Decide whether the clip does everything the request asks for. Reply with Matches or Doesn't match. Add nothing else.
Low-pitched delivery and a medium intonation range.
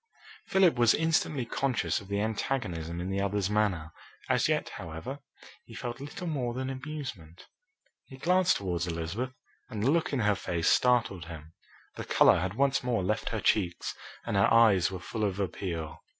Doesn't match